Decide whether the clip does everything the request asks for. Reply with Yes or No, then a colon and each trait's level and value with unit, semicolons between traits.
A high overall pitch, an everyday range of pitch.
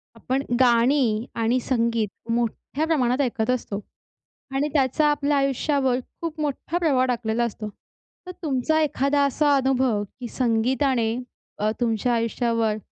Yes: very high, 255 Hz; average, 3.3 semitones